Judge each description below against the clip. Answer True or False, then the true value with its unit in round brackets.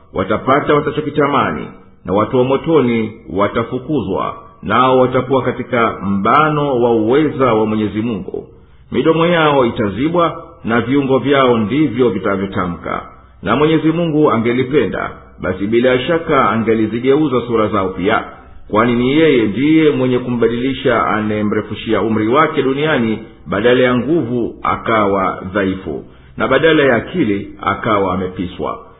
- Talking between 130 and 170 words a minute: False (115 wpm)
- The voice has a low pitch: True (120 Hz)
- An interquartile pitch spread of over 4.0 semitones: True (4.5 semitones)